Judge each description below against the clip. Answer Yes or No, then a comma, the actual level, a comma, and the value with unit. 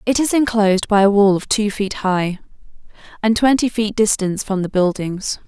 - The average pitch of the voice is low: No, high, 205 Hz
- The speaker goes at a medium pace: Yes, average, 185 wpm